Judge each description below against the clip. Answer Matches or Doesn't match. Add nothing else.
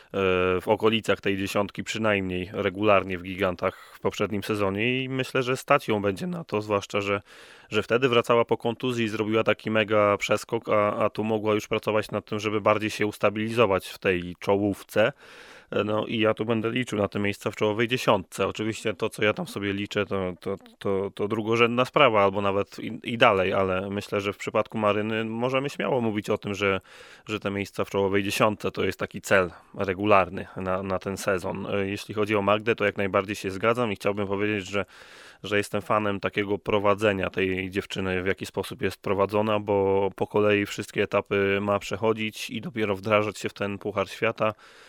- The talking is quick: Matches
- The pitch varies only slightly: Matches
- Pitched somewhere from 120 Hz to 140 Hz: Doesn't match